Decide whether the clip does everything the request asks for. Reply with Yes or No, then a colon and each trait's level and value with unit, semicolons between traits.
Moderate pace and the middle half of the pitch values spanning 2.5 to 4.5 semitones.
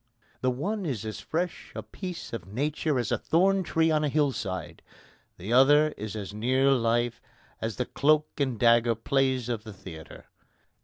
No: average, 175 wpm; average, 5.1 semitones